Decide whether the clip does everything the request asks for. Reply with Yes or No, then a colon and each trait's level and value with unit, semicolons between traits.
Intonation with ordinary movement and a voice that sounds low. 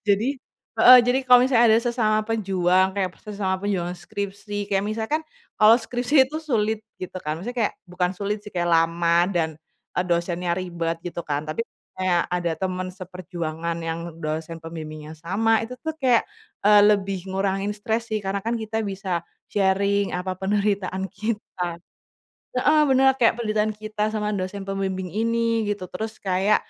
No: average, 3.5 semitones; high, 200 Hz